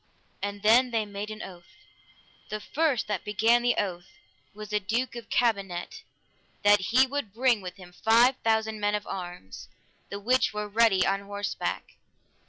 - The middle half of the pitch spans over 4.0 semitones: No, average, 2.7 semitones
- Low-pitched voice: No, high, 210 Hz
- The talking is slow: No, average, 165 wpm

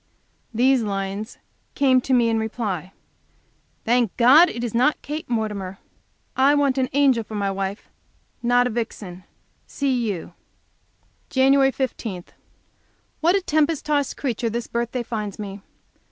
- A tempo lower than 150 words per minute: Yes, average, 140 wpm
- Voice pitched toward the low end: No, high, 235 Hz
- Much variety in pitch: No, average, 4.3 semitones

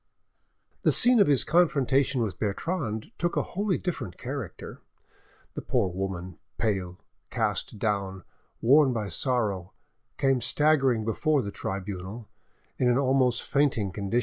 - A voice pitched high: No, low, 120 Hz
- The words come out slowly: Yes, slow, 130 wpm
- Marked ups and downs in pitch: Yes, wide, 6.1 semitones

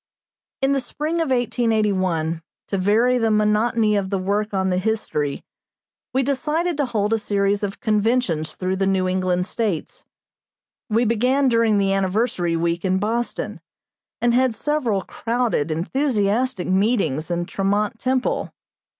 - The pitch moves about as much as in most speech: Yes, average, 4.3 semitones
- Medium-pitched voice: No, high, 210 Hz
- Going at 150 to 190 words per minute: No, average, 140 wpm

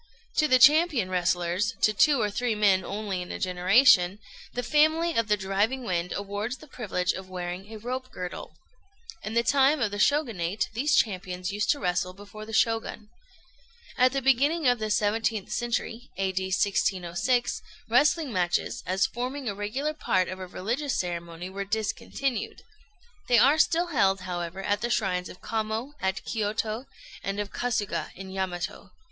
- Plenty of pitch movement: No, average, 4.9 semitones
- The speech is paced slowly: No, average, 165 wpm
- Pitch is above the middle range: Yes, high, 210 Hz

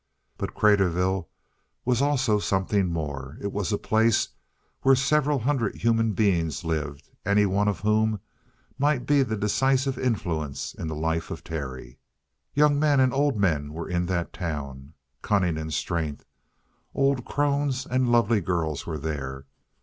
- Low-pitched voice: Yes, low, 100 Hz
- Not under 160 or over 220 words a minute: No, average, 150 wpm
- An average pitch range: No, wide, 7.9 semitones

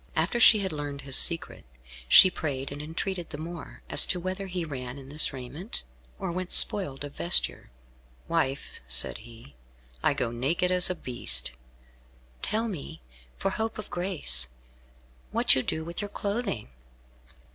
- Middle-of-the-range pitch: Yes, medium, 160 Hz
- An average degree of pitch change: No, wide, 5.8 semitones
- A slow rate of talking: No, average, 155 wpm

